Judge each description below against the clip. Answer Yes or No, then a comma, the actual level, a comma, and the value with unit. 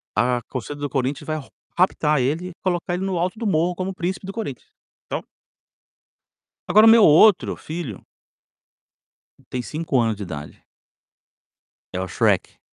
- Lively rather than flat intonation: Yes, wide, 6.3 semitones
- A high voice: No, medium, 160 Hz